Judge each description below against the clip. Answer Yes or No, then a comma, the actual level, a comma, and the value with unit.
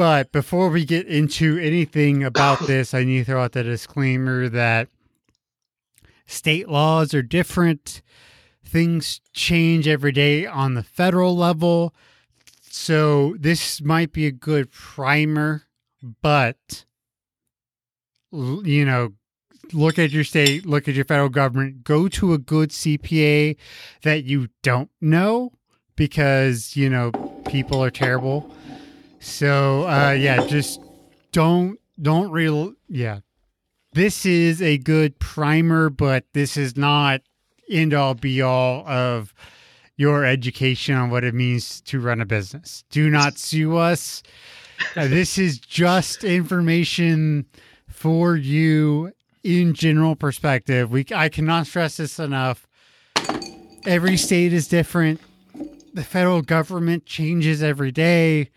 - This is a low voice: No, medium, 150 Hz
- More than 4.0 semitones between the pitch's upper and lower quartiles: No, average, 3.7 semitones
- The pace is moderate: No, slow, 125 wpm